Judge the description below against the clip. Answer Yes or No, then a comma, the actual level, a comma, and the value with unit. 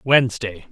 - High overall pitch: No, low, 115 Hz